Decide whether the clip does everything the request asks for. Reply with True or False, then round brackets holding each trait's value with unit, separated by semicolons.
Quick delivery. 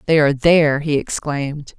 False (170 wpm)